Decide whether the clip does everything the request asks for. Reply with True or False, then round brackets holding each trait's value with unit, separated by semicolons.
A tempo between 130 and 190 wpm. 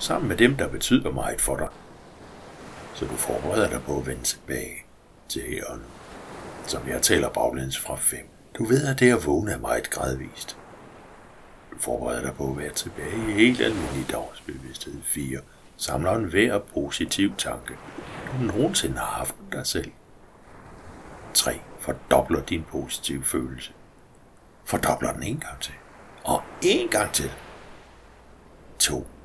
True (145 wpm)